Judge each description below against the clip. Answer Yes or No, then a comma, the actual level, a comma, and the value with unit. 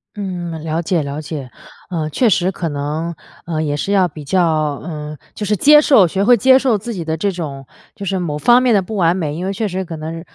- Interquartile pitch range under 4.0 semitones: No, average, 4.3 semitones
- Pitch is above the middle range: No, medium, 175 Hz